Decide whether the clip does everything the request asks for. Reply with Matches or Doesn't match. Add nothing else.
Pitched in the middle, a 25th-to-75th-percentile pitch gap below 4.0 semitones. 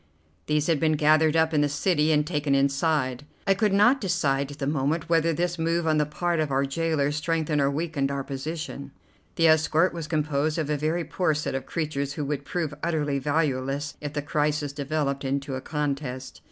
Matches